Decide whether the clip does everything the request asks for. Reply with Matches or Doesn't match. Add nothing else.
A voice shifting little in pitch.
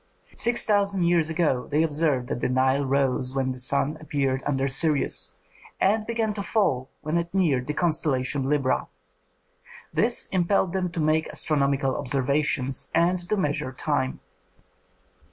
Doesn't match